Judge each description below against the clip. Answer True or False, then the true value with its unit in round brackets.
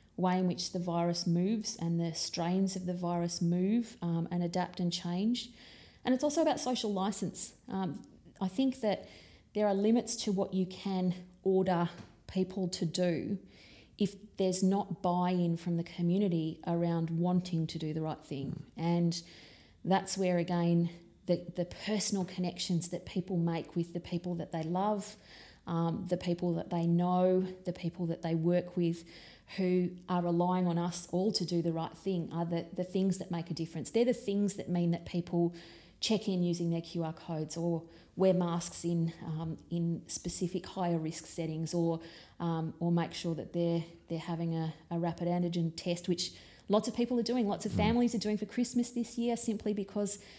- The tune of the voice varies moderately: False (2.1 semitones)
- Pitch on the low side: False (175 Hz)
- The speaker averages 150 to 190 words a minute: True (185 wpm)